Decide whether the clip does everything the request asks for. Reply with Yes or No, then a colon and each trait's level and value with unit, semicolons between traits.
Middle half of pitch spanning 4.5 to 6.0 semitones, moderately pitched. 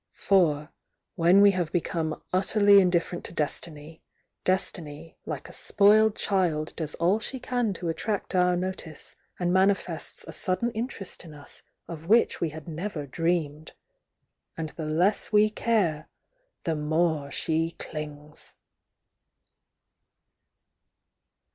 No: average, 3.9 semitones; medium, 170 Hz